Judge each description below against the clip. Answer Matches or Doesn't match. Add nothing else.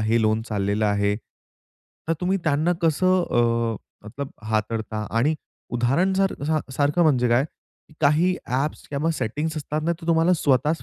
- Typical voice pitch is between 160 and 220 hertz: Doesn't match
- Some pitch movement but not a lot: Doesn't match